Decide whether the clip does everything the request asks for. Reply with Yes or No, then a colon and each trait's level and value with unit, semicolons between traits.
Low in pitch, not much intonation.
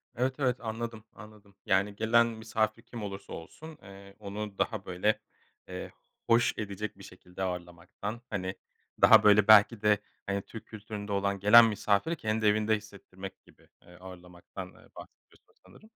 Yes: low, 105 Hz; narrow, 2.2 semitones